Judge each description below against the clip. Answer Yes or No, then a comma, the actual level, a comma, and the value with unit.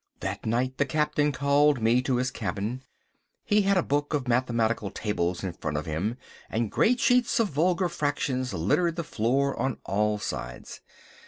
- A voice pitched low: Yes, low, 130 Hz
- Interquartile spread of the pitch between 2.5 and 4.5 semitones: No, wide, 5.6 semitones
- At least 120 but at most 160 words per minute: No, average, 170 wpm